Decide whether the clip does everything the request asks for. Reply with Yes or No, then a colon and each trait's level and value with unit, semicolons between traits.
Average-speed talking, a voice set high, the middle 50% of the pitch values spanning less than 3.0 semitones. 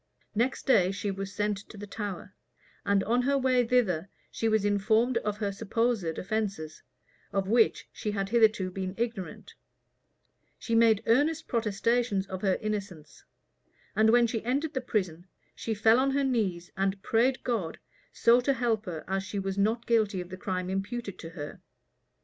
No: average, 170 wpm; high, 210 Hz; average, 3.5 semitones